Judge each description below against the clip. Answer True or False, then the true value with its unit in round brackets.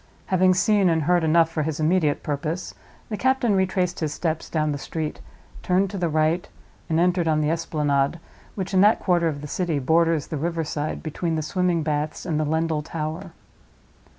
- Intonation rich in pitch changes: False (2.7 semitones)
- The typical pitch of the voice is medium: True (165 Hz)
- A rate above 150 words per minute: True (185 wpm)